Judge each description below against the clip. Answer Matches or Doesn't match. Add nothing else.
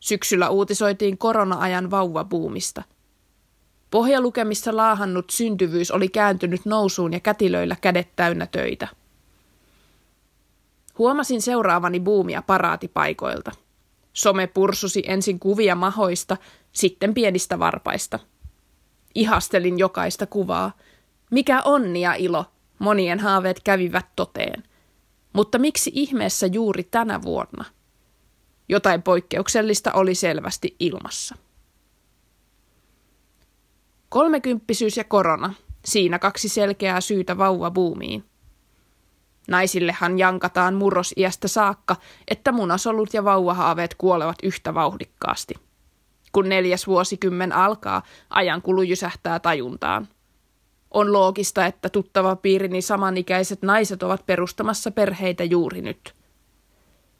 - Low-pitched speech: Doesn't match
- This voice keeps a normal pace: Doesn't match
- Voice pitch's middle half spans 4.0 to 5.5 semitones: Doesn't match